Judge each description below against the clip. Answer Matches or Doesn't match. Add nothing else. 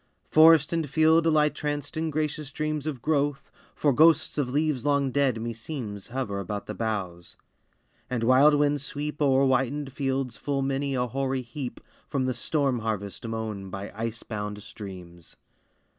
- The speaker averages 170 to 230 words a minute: Doesn't match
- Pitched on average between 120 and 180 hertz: Matches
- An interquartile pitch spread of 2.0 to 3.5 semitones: Doesn't match